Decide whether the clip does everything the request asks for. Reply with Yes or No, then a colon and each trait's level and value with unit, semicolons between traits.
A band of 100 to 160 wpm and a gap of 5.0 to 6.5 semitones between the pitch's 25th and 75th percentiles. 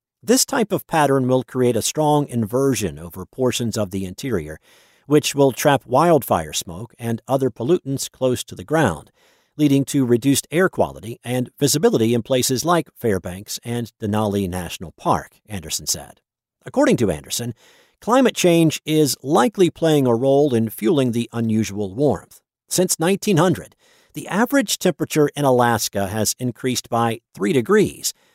Yes: average, 150 wpm; average, 5.3 semitones